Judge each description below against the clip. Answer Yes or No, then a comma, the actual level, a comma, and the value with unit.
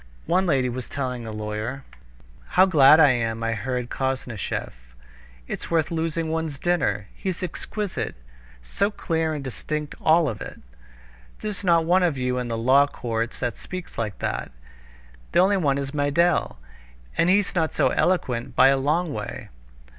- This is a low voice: No, medium, 145 Hz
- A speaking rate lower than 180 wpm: Yes, average, 160 wpm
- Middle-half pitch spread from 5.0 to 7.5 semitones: Yes, wide, 5.5 semitones